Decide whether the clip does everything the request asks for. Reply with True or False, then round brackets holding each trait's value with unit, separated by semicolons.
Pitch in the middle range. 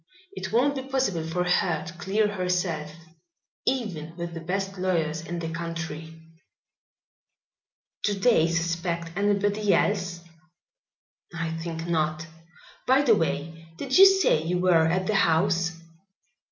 True (175 Hz)